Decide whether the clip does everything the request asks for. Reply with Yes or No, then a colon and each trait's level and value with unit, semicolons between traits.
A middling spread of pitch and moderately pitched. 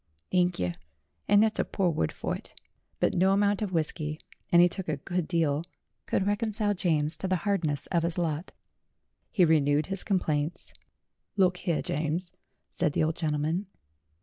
Yes: average, 3.7 semitones; medium, 175 Hz